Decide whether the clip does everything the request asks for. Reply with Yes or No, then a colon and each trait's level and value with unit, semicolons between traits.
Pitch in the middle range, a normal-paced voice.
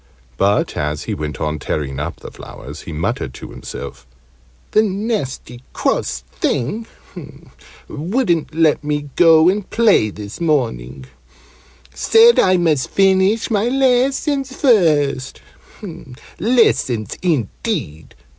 No: medium, 160 Hz; slow, 110 wpm